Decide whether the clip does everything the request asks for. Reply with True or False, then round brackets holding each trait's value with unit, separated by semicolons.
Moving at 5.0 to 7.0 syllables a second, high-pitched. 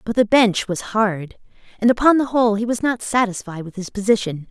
True (5.5 syllables/s; 215 Hz)